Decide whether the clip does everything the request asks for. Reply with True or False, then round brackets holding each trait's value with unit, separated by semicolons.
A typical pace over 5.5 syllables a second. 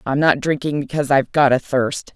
True (5.9 syllables/s)